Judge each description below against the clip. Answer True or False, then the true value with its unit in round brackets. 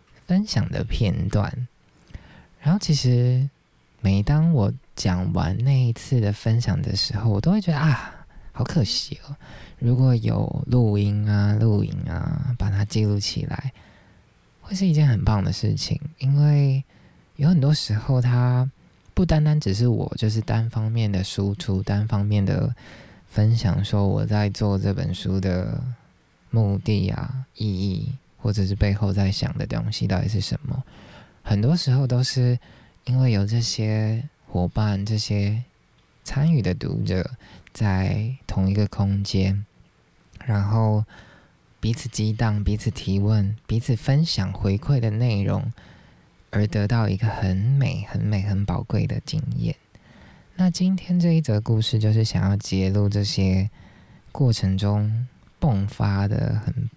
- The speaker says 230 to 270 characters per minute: False (205 characters per minute)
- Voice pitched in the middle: False (110 Hz)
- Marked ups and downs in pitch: False (4.6 semitones)